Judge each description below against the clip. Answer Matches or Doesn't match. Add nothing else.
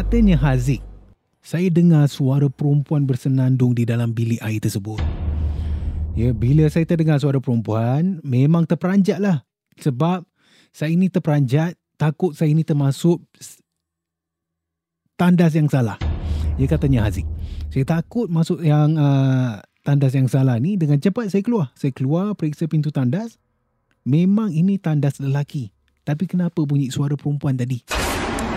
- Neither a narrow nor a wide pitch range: Doesn't match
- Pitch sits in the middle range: Matches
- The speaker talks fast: Doesn't match